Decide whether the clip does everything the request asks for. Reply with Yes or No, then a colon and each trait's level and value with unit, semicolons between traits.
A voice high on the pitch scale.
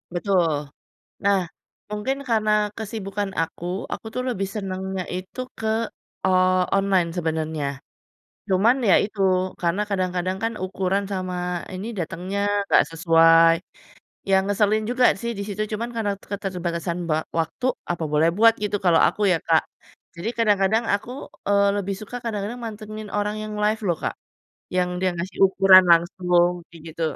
Yes: high, 195 Hz